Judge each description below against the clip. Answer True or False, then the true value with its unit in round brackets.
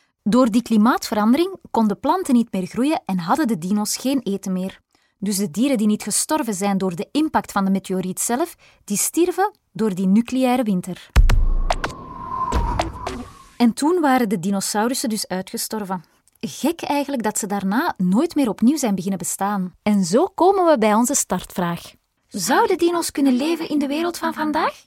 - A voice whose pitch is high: True (230 Hz)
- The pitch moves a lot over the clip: True (6.8 semitones)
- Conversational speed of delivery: True (165 wpm)